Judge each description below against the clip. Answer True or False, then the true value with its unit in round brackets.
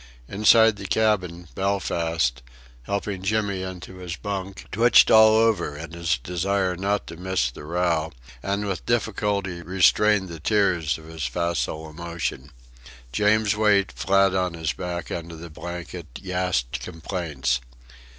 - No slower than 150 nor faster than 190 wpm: False (140 wpm)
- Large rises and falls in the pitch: False (3.2 semitones)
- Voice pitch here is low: True (90 Hz)